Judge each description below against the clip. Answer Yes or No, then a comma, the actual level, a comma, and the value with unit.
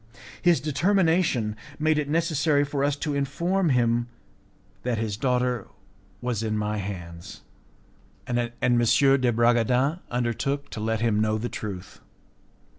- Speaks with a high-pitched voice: No, low, 125 Hz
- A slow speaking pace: Yes, slow, 130 wpm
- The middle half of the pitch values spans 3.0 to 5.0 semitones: Yes, average, 4.4 semitones